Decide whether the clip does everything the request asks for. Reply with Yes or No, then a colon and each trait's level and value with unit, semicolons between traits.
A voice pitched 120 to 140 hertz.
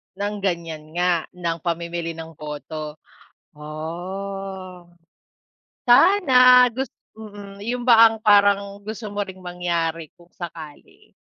No: medium, 185 Hz